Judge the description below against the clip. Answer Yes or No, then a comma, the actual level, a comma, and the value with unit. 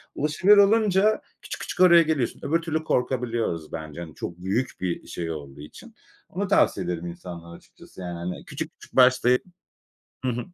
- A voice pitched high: No, low, 120 Hz